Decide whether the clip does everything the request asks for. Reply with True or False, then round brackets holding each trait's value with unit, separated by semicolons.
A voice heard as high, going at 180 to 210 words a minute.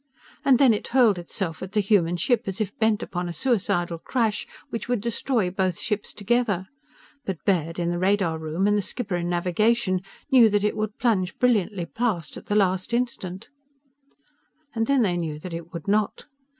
True (200 Hz; 190 wpm)